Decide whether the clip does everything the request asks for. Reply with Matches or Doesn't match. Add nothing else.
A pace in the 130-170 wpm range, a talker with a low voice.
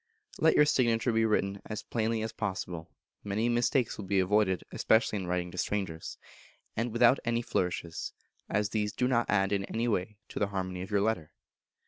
Doesn't match